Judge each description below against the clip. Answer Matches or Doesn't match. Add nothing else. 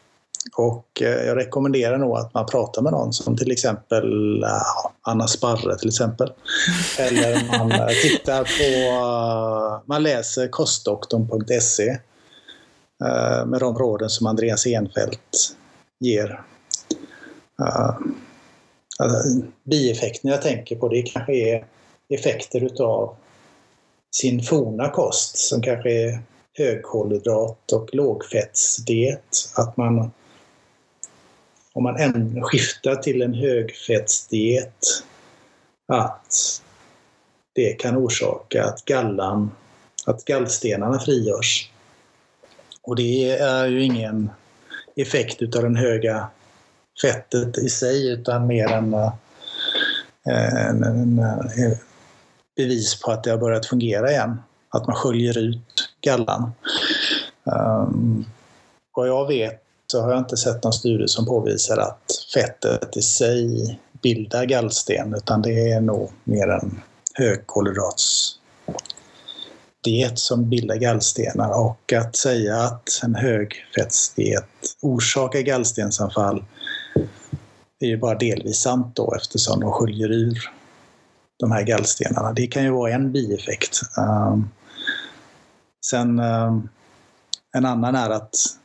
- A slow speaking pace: Matches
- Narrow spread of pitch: Matches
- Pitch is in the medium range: Doesn't match